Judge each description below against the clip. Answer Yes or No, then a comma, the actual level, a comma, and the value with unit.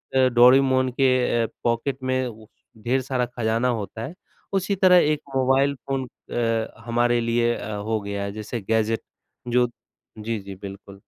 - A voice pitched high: No, low, 120 Hz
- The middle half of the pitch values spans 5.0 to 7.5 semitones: No, average, 2.8 semitones